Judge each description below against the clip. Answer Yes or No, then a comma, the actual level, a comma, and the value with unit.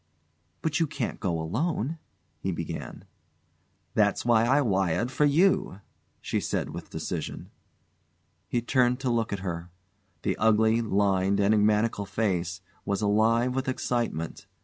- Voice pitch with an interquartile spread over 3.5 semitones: Yes, average, 4.5 semitones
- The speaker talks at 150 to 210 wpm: No, slow, 135 wpm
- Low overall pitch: Yes, low, 110 Hz